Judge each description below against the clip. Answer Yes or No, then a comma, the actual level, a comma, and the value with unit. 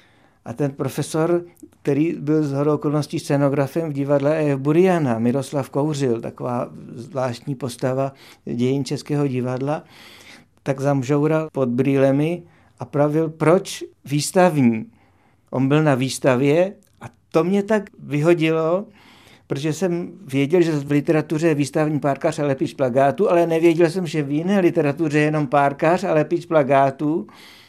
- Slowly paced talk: No, average, 135 wpm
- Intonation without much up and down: No, average, 3.0 semitones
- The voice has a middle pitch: Yes, medium, 145 Hz